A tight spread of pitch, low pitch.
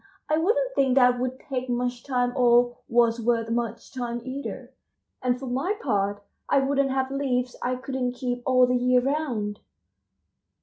No: narrow, 1.8 semitones; very high, 250 Hz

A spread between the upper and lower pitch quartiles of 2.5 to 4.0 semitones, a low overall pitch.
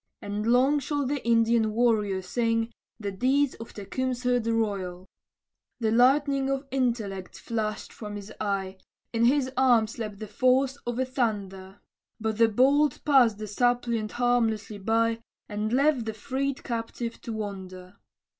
No: average, 3.3 semitones; high, 230 Hz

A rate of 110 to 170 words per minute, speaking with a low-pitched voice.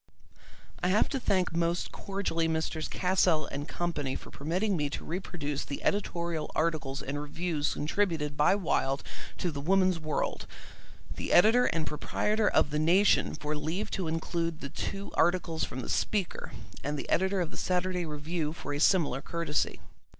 No: average, 165 wpm; medium, 165 Hz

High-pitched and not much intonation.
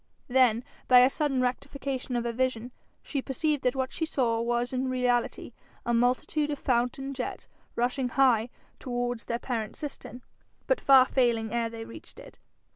Yes: very high, 250 Hz; narrow, 1.9 semitones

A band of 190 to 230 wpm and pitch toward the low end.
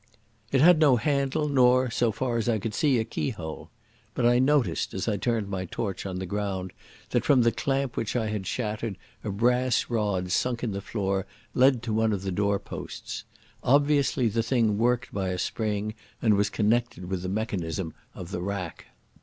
Yes: average, 195 wpm; low, 110 Hz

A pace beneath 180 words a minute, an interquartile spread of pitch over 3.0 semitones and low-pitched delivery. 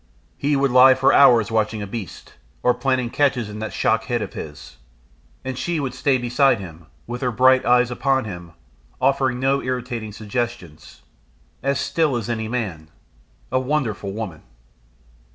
Yes: average, 160 wpm; average, 3.6 semitones; low, 120 Hz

